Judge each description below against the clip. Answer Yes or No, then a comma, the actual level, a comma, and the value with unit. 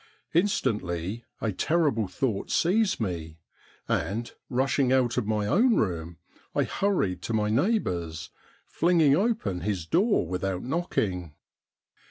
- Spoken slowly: Yes, slow, 120 wpm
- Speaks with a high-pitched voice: No, low, 110 Hz